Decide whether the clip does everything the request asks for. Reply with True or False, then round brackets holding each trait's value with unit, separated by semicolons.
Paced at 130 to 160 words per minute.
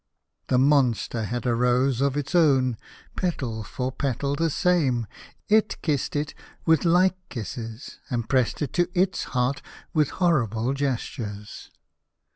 True (135 wpm)